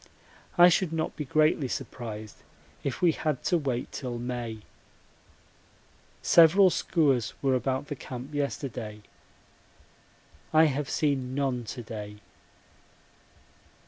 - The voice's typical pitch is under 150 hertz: Yes, low, 135 Hz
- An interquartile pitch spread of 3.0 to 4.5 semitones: Yes, average, 4.2 semitones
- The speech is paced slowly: Yes, slow, 110 wpm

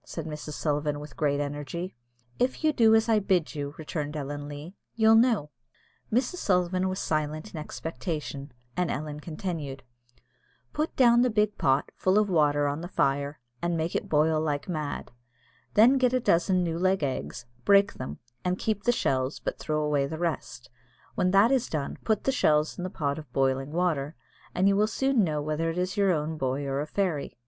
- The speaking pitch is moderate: Yes, medium, 160 Hz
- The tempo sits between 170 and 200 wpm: Yes, average, 195 wpm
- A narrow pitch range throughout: No, average, 5.2 semitones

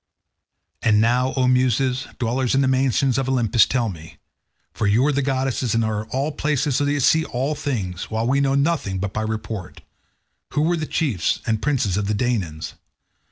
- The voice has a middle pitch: No, low, 125 Hz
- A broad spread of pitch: No, average, 4.0 semitones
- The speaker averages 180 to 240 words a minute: Yes, average, 185 wpm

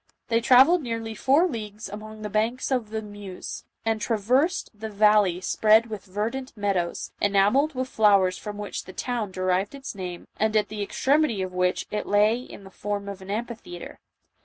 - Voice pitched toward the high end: Yes, high, 215 Hz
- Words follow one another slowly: No, average, 180 wpm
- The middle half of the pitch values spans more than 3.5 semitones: No, average, 2.7 semitones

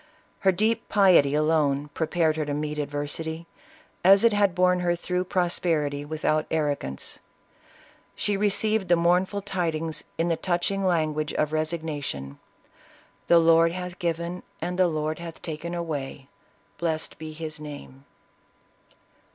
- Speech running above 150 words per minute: No, slow, 135 wpm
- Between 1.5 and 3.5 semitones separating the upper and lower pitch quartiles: Yes, average, 2.9 semitones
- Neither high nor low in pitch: Yes, medium, 165 Hz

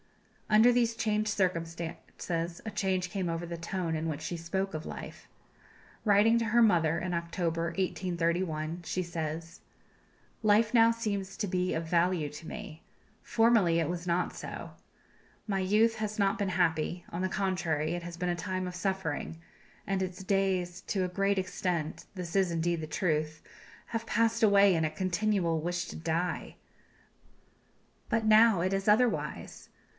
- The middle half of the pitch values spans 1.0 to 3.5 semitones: Yes, average, 3.2 semitones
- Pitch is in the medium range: Yes, medium, 180 Hz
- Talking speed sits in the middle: Yes, average, 160 wpm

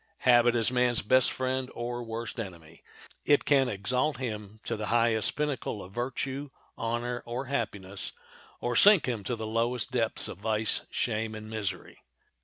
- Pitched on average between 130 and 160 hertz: No, low, 120 Hz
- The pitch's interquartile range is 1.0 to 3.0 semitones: Yes, average, 2.7 semitones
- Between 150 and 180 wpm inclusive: Yes, average, 160 wpm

